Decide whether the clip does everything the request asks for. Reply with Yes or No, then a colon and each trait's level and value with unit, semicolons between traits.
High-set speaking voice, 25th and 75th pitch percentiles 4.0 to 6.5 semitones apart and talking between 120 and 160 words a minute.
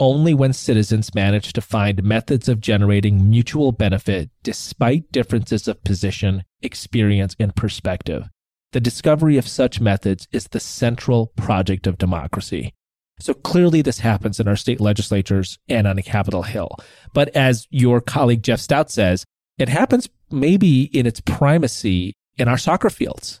No: low, 110 Hz; average, 4.6 semitones; average, 150 wpm